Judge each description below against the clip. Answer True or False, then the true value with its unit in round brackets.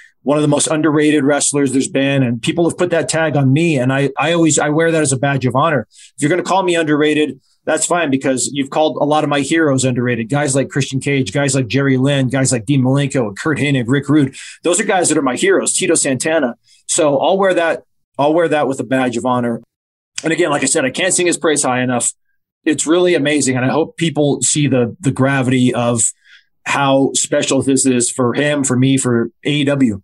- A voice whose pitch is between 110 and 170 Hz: True (140 Hz)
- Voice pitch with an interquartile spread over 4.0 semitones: False (2.9 semitones)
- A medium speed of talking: False (235 wpm)